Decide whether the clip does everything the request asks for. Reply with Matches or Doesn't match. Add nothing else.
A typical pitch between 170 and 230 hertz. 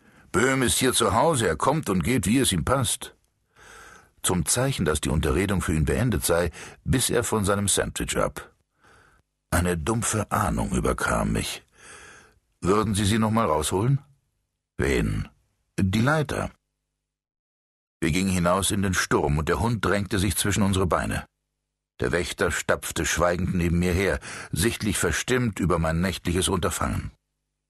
Doesn't match